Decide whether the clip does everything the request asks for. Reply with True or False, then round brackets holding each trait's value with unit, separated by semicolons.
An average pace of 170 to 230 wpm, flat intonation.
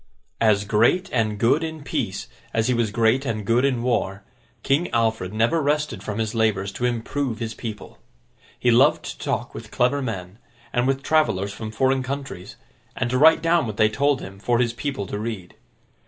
False (190 wpm; 4.1 semitones)